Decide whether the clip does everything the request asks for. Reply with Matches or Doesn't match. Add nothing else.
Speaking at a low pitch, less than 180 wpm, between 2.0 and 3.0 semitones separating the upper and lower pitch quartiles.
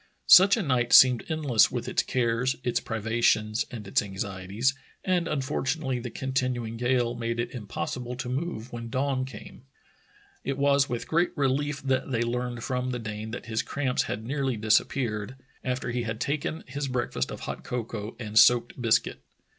Matches